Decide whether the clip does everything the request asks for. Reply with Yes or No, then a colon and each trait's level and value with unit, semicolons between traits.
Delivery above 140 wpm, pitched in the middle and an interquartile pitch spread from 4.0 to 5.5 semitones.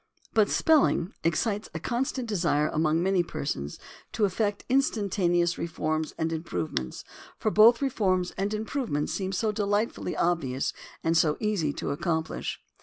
No: slow, 135 wpm; medium, 180 Hz; average, 5.0 semitones